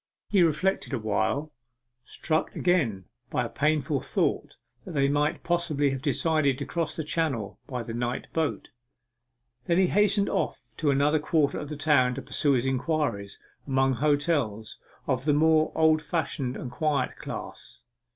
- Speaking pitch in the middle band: Yes, medium, 145 Hz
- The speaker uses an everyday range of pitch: Yes, average, 3.4 semitones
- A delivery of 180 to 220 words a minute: No, average, 155 wpm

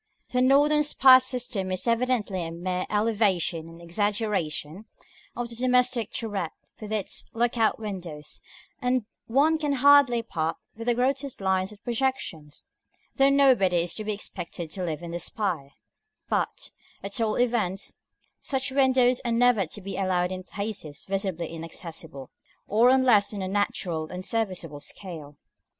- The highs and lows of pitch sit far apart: Yes, wide, 5.7 semitones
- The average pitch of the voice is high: Yes, high, 210 Hz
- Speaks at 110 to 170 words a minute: Yes, average, 155 wpm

